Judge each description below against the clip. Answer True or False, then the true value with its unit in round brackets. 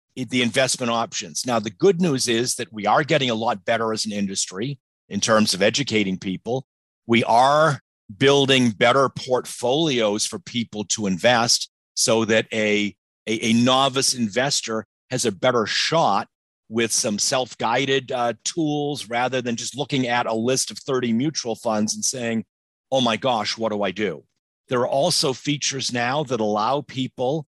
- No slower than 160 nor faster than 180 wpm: True (165 wpm)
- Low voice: True (120 Hz)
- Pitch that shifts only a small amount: False (3.2 semitones)